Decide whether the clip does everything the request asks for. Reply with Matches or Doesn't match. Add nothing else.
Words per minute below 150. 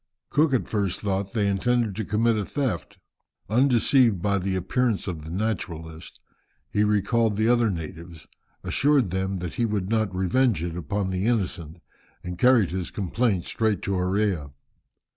Doesn't match